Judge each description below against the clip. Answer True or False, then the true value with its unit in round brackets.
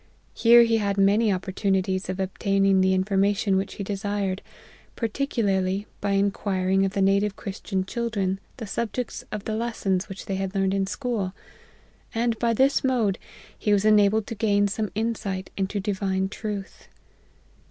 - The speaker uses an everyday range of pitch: False (2.2 semitones)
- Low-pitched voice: False (200 Hz)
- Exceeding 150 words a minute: True (160 wpm)